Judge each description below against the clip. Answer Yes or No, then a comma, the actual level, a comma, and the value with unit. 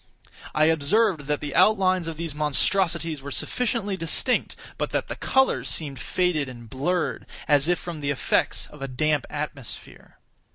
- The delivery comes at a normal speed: Yes, average, 160 wpm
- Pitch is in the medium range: Yes, medium, 155 Hz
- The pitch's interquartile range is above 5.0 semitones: No, average, 4.2 semitones